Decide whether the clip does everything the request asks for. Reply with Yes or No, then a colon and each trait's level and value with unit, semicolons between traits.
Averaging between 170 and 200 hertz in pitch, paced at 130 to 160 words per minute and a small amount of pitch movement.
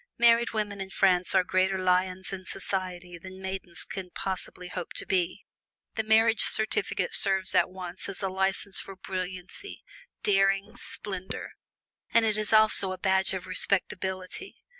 Yes: high, 190 Hz; average, 150 wpm; narrow, 1.7 semitones